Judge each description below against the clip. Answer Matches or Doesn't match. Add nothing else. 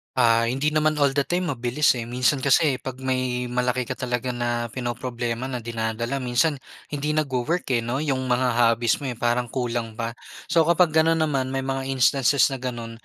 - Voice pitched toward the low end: Matches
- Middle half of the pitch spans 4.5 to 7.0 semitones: Doesn't match